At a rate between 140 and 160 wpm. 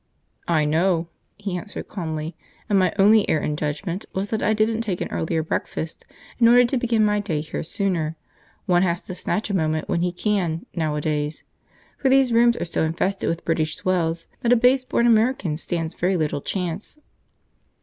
No: average, 185 wpm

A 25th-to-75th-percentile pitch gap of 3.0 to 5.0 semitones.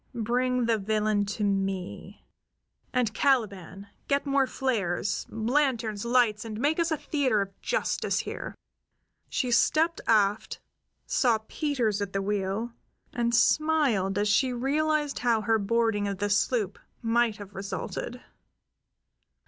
Yes: average, 3.9 semitones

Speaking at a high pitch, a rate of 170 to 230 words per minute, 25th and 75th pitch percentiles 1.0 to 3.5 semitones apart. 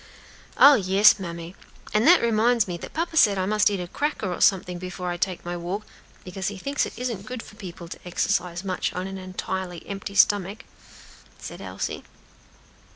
Yes: high, 195 Hz; average, 185 wpm; average, 2.9 semitones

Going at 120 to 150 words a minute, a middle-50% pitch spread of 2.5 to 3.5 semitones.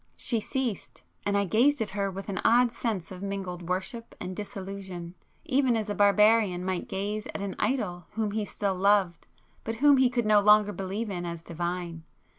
No: average, 185 wpm; average, 3.1 semitones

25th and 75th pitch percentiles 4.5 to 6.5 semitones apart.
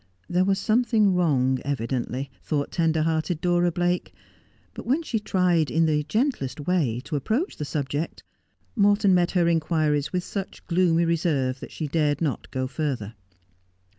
No: average, 4.1 semitones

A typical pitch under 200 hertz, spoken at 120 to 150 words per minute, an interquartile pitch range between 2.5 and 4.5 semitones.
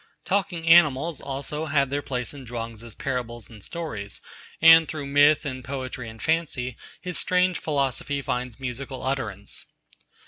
Yes: low, 135 Hz; average, 145 wpm; average, 4.0 semitones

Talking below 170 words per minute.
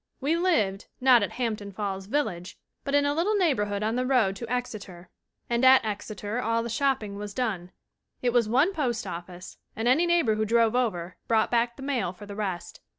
No: average, 200 wpm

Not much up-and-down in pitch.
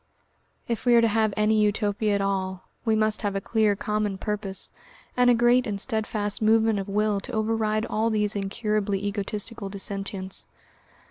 Yes: narrow, 1.7 semitones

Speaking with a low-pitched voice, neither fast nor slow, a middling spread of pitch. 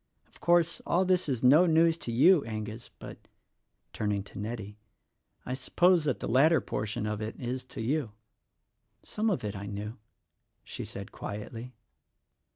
No: low, 125 Hz; average, 160 wpm; wide, 7.2 semitones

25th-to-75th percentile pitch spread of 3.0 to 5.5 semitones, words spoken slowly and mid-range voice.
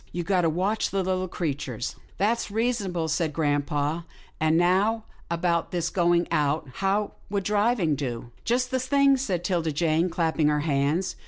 No: average, 4.4 semitones; average, 175 wpm; medium, 175 Hz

